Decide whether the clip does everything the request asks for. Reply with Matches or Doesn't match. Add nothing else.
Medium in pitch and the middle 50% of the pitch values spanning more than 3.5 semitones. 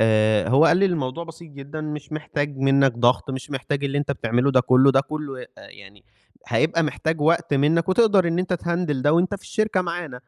Matches